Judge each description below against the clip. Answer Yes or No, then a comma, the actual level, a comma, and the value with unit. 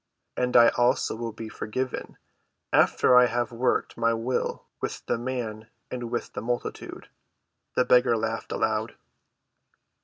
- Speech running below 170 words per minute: Yes, average, 140 wpm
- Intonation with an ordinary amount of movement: No, narrow, 1.6 semitones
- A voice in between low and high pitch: No, low, 120 Hz